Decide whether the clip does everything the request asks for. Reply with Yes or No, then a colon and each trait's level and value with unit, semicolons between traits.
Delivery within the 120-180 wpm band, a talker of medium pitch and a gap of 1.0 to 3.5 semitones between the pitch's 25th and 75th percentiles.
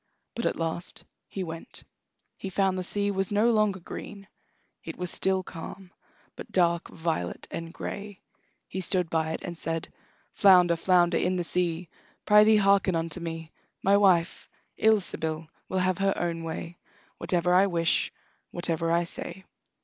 Yes: average, 155 wpm; medium, 180 Hz; narrow, 2.6 semitones